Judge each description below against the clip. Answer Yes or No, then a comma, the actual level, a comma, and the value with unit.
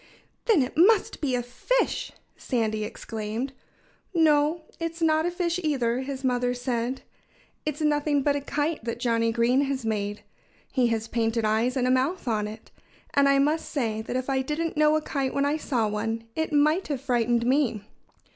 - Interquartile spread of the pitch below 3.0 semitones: No, average, 4.5 semitones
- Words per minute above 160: Yes, average, 185 wpm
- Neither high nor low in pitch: No, very high, 265 Hz